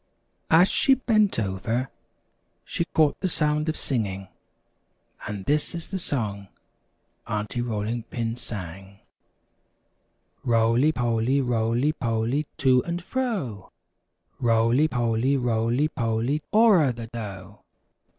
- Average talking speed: No, slow, 110 wpm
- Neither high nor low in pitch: No, low, 120 Hz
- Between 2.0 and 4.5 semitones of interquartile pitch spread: No, average, 5.2 semitones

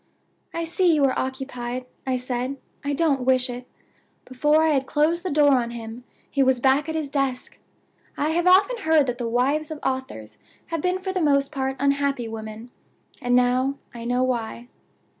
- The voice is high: Yes, very high, 270 Hz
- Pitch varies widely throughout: No, average, 3.5 semitones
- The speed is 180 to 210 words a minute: Yes, average, 185 wpm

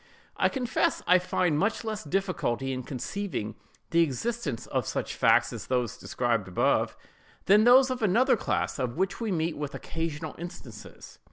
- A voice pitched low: No, medium, 170 Hz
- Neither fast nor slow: Yes, average, 160 wpm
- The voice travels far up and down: Yes, wide, 8.3 semitones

